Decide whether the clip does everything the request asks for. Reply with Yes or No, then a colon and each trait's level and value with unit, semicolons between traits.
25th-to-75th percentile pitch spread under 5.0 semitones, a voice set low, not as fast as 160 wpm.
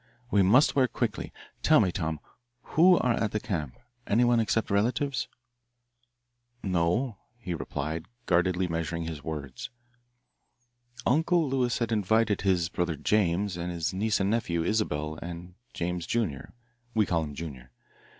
No: average, 5.3 semitones; very low, 90 Hz; average, 140 wpm